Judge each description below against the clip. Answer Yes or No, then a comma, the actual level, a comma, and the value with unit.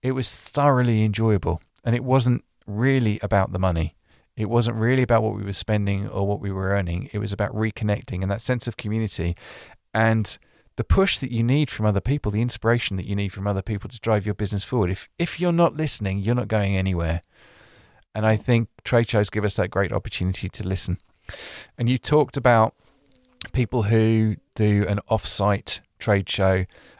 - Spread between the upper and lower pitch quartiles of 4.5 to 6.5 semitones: No, average, 3.3 semitones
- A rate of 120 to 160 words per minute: No, average, 195 wpm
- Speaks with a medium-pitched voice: No, low, 110 Hz